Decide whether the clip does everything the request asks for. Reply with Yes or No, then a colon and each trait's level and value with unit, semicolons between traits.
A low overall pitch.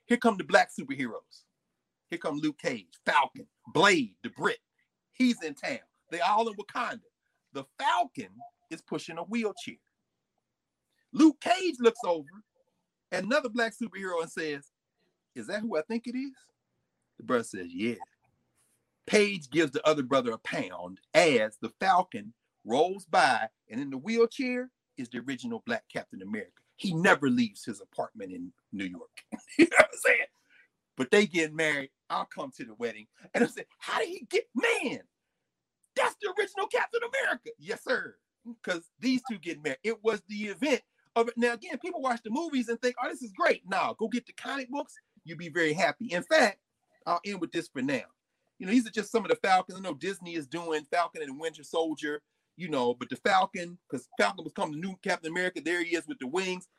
No: high, 230 Hz